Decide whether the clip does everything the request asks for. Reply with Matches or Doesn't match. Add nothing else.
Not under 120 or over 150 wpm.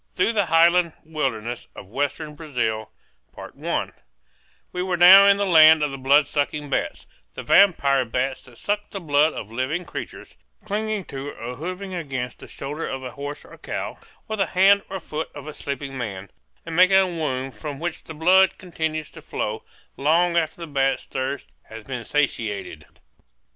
Doesn't match